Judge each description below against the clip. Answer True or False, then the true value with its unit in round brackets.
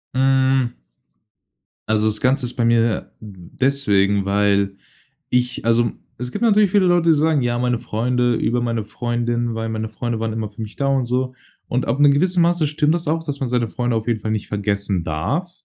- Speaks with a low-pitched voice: True (120 Hz)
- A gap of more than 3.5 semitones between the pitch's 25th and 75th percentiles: True (3.9 semitones)